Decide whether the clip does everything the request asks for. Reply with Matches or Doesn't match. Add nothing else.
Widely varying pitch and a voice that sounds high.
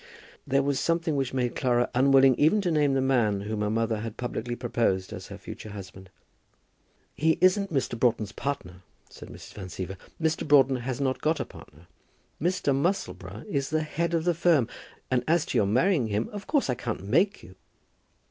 Doesn't match